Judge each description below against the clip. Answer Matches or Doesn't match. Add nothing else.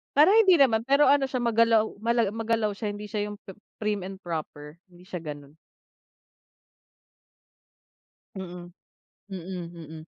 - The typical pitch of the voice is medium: Doesn't match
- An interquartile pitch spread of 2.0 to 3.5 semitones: Doesn't match